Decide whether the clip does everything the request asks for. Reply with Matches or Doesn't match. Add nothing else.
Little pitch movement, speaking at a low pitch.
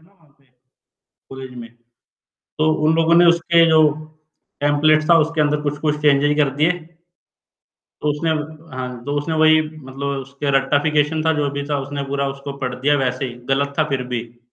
Doesn't match